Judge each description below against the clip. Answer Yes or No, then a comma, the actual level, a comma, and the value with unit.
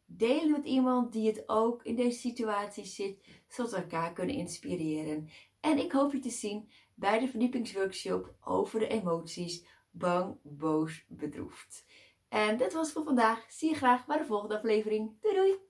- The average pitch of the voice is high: Yes, high, 220 Hz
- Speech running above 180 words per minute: No, average, 170 wpm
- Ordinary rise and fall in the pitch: No, wide, 5.7 semitones